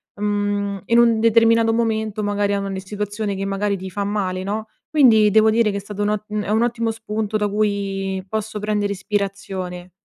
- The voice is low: No, high, 205 Hz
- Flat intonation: Yes, narrow, 1.7 semitones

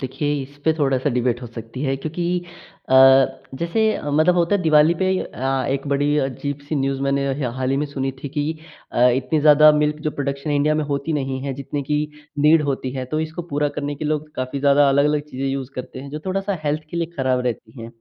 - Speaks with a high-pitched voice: No, medium, 145 Hz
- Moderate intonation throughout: No, narrow, 2.2 semitones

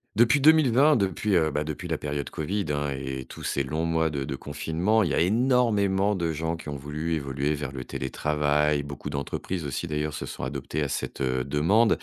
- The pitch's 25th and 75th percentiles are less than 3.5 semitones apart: No, average, 5.0 semitones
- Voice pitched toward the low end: Yes, very low, 75 Hz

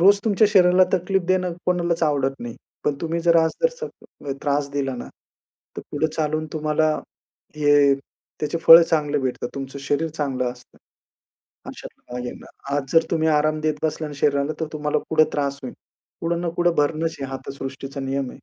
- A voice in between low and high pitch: Yes, medium, 155 Hz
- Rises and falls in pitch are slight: No, average, 3.0 semitones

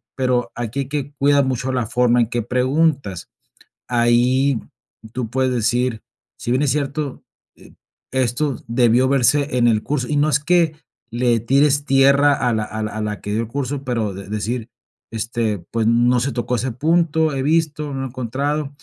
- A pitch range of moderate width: Yes, average, 3.2 semitones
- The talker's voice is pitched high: No, low, 125 Hz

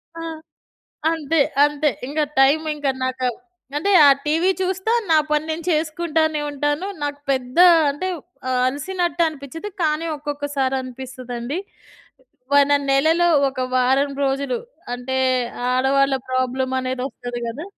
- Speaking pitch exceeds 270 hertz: Yes, very high, 285 Hz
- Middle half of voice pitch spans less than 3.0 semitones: No, average, 3.4 semitones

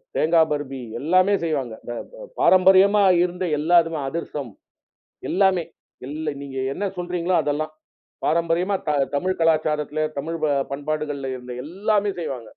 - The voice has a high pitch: No, medium, 165 Hz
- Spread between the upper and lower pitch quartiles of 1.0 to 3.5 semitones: No, average, 3.9 semitones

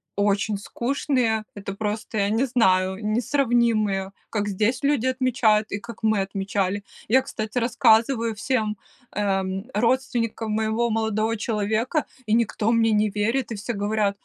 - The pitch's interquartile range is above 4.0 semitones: No, narrow, 2.4 semitones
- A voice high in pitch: Yes, high, 220 Hz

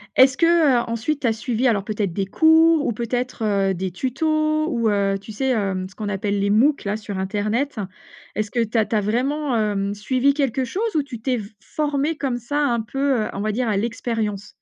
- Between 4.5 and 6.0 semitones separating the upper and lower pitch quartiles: Yes, average, 4.9 semitones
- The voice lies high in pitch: Yes, high, 235 Hz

